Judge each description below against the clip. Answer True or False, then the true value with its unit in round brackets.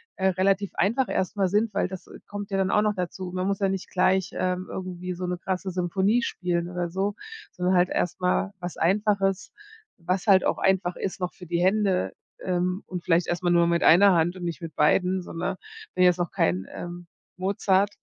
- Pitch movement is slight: True (1.7 semitones)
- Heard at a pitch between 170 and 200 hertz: True (185 Hz)